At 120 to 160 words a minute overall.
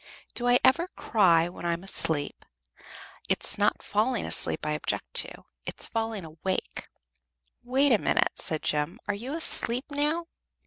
Yes: average, 150 wpm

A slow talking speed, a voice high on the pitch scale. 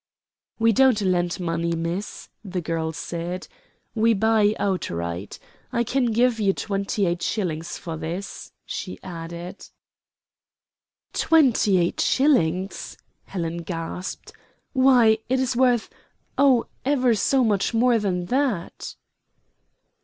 Yes: slow, 115 wpm; high, 195 Hz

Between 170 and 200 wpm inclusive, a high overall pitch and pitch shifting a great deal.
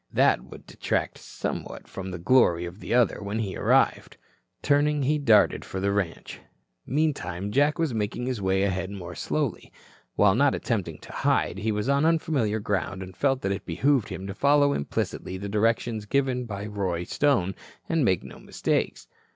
No: average, 175 wpm; low, 105 Hz; wide, 6.3 semitones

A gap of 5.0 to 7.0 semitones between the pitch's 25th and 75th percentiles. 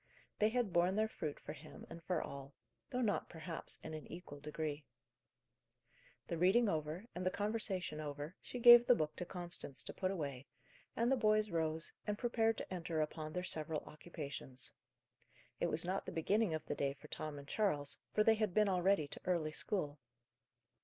Yes: average, 5.3 semitones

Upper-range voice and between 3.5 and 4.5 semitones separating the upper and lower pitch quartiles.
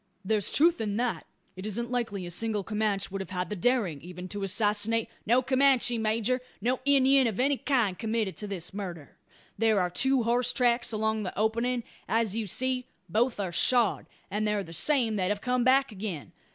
Yes: high, 220 Hz; average, 3.8 semitones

